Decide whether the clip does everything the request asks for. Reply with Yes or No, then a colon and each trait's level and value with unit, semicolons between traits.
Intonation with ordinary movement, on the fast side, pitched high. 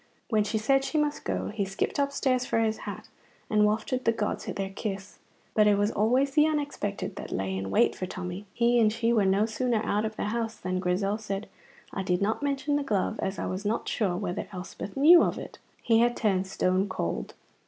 Yes: average, 3.6 semitones; fast, 215 wpm; high, 215 Hz